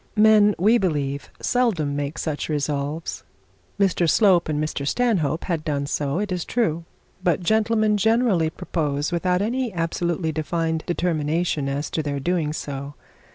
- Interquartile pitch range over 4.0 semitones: Yes, average, 5.0 semitones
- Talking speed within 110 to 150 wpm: Yes, average, 145 wpm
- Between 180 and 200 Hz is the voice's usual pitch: No, medium, 165 Hz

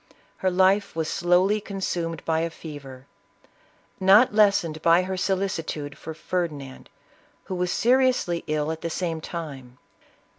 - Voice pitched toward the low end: No, medium, 170 Hz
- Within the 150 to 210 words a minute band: No, average, 140 wpm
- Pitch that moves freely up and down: No, average, 3.3 semitones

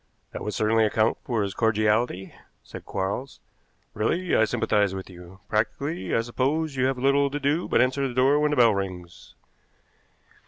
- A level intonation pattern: No, average, 4.9 semitones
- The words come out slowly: No, average, 170 wpm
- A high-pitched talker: No, low, 115 Hz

